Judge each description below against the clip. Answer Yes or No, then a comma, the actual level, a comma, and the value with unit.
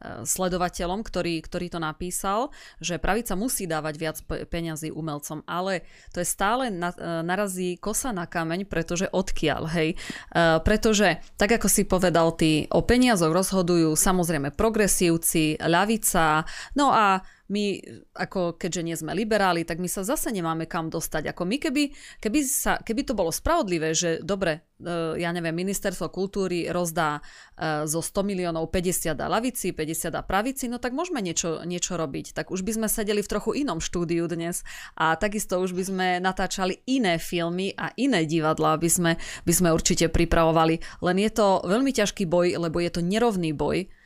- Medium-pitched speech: Yes, medium, 180 Hz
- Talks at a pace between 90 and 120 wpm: No, average, 160 wpm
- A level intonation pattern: No, average, 3.4 semitones